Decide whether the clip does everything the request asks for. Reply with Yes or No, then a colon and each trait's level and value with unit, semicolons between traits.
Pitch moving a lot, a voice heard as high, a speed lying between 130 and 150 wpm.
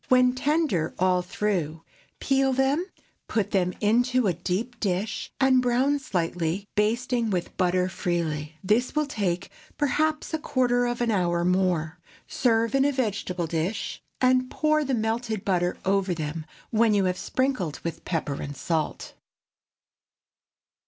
Yes: wide, 6.1 semitones; high, 210 Hz; average, 140 wpm